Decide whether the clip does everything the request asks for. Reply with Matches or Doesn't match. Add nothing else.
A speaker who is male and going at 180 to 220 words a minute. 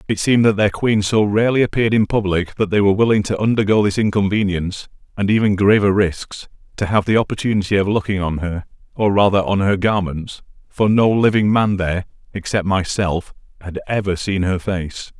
Matches